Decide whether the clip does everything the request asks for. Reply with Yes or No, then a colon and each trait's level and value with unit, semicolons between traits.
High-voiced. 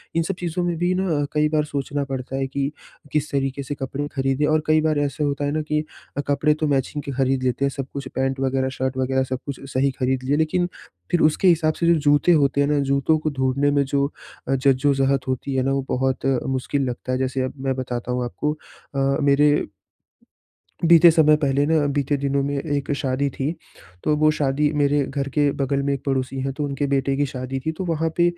No: medium, 140 Hz